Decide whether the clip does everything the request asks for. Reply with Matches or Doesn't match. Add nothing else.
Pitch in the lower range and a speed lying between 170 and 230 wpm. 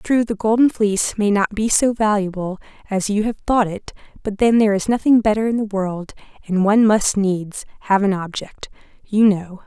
Doesn't match